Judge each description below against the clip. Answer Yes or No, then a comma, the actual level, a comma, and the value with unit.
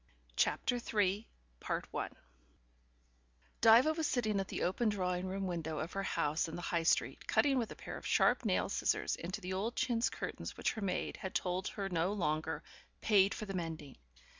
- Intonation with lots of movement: No, average, 3.7 semitones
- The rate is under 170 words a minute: No, average, 180 wpm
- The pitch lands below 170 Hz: No, high, 190 Hz